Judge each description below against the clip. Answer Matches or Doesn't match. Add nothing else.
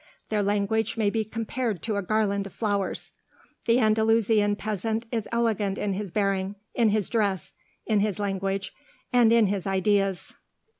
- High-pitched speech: Matches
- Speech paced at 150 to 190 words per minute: Matches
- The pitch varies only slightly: Matches